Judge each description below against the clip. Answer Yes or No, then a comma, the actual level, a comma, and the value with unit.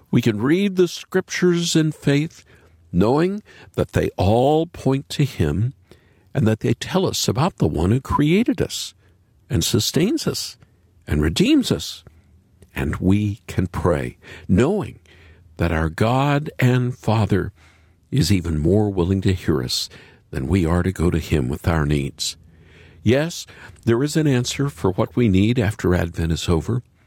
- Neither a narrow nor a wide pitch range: No, wide, 7.7 semitones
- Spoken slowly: No, average, 155 wpm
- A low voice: Yes, low, 100 Hz